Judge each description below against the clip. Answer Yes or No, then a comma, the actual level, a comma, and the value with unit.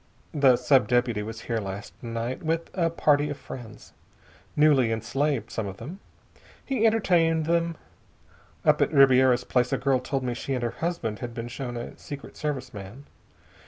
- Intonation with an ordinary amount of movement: Yes, average, 4.4 semitones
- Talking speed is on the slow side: No, average, 170 wpm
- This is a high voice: No, low, 130 Hz